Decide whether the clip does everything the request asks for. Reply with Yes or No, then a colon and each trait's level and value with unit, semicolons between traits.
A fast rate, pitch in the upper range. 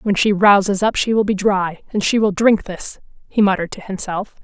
Yes: fast, 230 wpm; high, 200 Hz